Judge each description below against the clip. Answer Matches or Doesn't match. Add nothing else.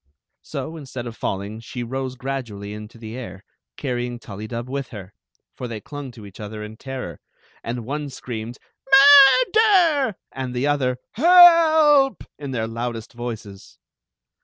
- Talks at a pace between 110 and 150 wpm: Matches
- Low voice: Matches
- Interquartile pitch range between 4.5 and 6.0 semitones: Matches